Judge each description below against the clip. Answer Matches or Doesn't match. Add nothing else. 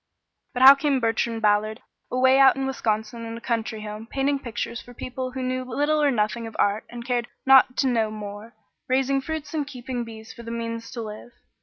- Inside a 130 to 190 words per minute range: Doesn't match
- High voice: Matches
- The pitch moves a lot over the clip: Doesn't match